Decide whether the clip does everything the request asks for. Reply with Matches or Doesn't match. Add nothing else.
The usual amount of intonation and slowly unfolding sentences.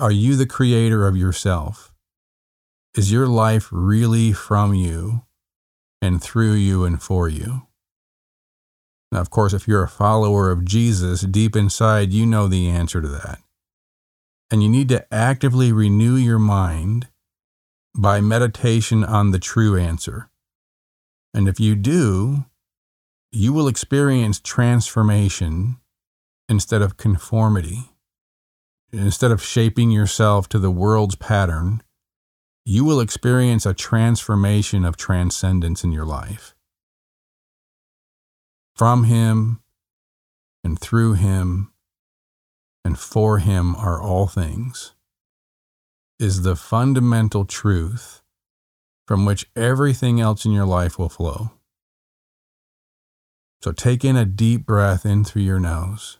Matches